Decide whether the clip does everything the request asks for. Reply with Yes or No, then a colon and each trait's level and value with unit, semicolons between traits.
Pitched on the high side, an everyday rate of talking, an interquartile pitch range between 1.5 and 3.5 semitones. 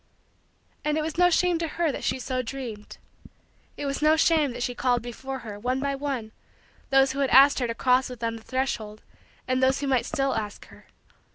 No: very high, 265 Hz; fast, 215 wpm; narrow, 2.6 semitones